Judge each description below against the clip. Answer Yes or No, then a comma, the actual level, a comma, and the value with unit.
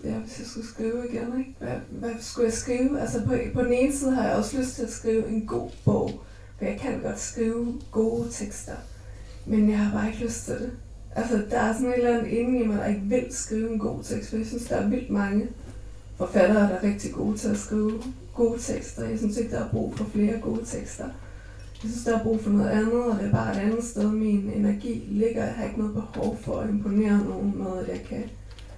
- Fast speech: Yes, fast, 245 wpm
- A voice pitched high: Yes, high, 220 Hz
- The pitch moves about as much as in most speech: No, narrow, 2.3 semitones